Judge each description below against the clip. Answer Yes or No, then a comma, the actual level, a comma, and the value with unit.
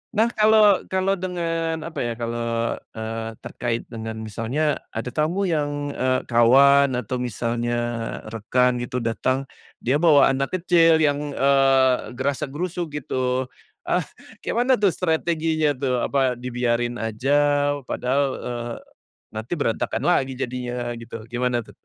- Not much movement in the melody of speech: No, average, 4.4 semitones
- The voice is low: Yes, low, 130 Hz